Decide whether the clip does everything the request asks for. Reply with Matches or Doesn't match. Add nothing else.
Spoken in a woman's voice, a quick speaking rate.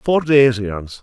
Doesn't match